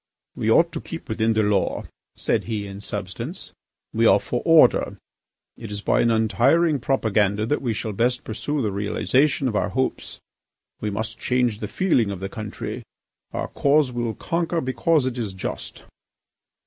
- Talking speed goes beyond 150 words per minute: Yes, average, 170 wpm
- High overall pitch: No, low, 115 Hz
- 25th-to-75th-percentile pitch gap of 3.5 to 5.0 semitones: Yes, average, 3.9 semitones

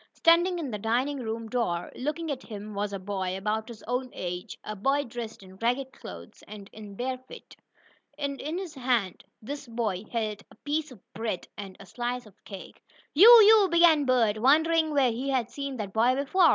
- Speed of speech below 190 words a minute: No, average, 195 wpm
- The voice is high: Yes, high, 245 Hz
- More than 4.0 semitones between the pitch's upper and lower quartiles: Yes, average, 5.1 semitones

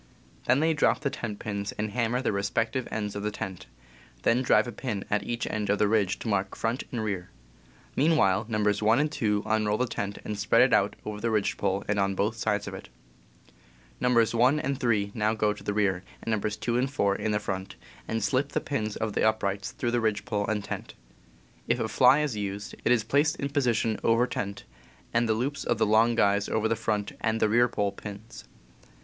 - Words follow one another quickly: Yes, fast, 225 wpm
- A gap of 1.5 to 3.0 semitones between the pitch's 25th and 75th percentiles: Yes, narrow, 2.6 semitones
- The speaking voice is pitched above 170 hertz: No, low, 110 Hz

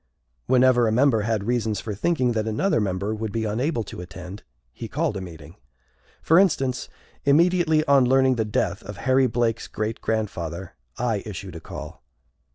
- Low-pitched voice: Yes, low, 110 Hz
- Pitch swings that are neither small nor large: Yes, average, 4.2 semitones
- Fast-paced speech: No, average, 165 wpm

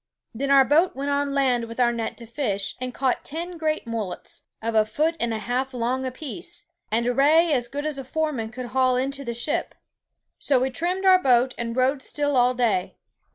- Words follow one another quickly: Yes, fast, 210 wpm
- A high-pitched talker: Yes, very high, 260 Hz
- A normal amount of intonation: Yes, average, 3.4 semitones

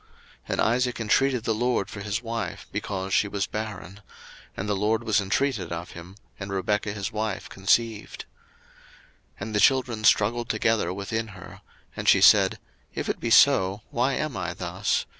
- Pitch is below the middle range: Yes, low, 105 Hz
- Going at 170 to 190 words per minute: Yes, average, 175 wpm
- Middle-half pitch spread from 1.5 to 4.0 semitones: Yes, average, 2.9 semitones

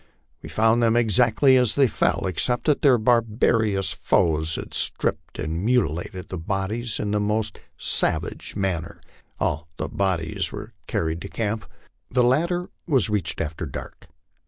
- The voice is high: No, low, 105 Hz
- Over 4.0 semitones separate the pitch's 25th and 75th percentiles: Yes, average, 5.0 semitones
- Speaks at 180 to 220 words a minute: No, average, 150 wpm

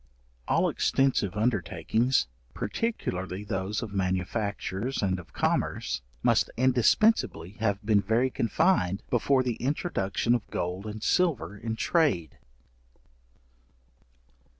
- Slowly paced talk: Yes, slow, 105 wpm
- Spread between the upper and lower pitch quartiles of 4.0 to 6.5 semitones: Yes, average, 5.2 semitones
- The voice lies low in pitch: Yes, low, 105 Hz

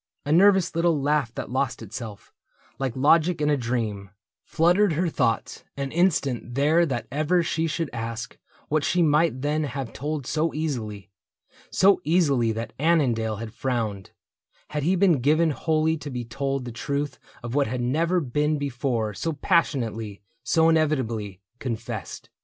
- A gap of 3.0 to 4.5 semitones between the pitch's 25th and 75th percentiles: No, average, 5.2 semitones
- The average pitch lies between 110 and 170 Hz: Yes, medium, 140 Hz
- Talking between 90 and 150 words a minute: No, average, 160 wpm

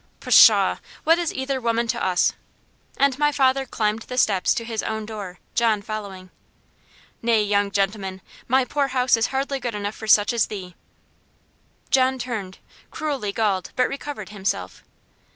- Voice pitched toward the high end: Yes, high, 225 Hz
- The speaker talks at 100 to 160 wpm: Yes, average, 155 wpm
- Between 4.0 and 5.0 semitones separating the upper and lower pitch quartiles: Yes, average, 4.4 semitones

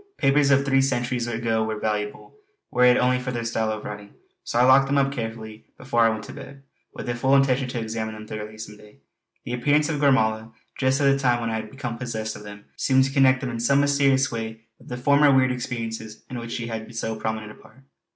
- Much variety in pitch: No, average, 3.3 semitones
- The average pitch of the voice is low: Yes, low, 120 Hz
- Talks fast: Yes, fast, 240 wpm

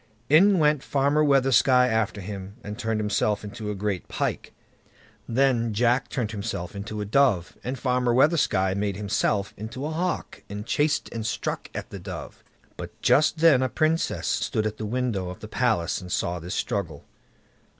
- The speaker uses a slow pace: No, average, 170 wpm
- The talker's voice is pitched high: No, low, 110 Hz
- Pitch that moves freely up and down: No, average, 4.8 semitones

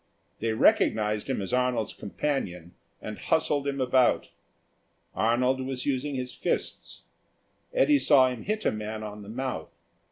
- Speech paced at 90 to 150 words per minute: Yes, average, 140 wpm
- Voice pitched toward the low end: Yes, low, 125 Hz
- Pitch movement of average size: Yes, average, 4.0 semitones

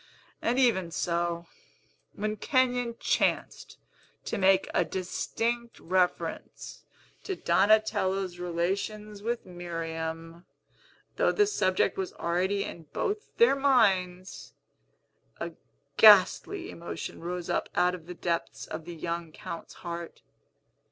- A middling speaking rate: No, slow, 110 wpm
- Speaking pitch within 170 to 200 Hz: Yes, medium, 185 Hz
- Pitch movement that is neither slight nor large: Yes, average, 4.1 semitones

